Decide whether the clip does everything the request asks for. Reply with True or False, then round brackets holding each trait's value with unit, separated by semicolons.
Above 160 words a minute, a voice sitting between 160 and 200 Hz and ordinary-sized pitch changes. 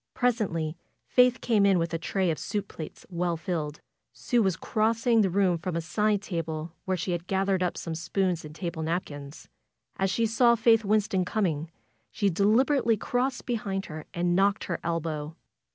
True (180 wpm; 185 Hz; 4.3 semitones)